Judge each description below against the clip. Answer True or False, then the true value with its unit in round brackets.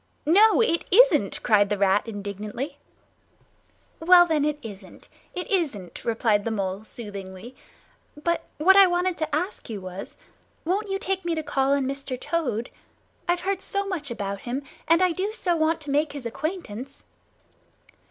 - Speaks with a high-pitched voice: True (290 Hz)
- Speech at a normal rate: True (160 wpm)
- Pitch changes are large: True (8.5 semitones)